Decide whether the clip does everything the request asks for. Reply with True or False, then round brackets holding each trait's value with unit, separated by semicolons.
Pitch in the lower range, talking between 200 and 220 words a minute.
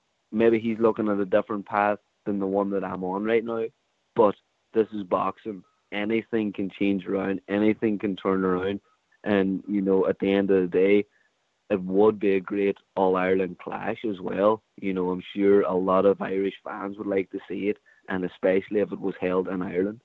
True (100 Hz; 205 wpm)